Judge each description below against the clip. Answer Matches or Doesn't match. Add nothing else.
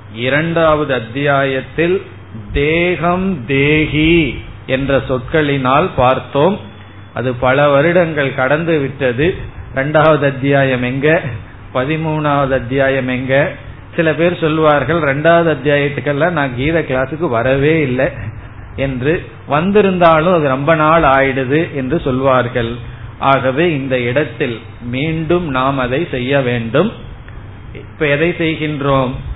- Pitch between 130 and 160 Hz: Matches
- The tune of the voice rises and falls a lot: Doesn't match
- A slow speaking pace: Doesn't match